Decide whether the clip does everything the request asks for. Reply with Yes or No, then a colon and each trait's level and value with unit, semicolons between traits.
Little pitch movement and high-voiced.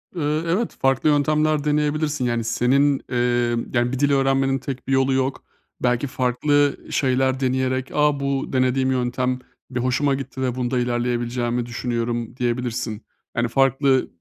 No: narrow, 2.2 semitones; low, 130 Hz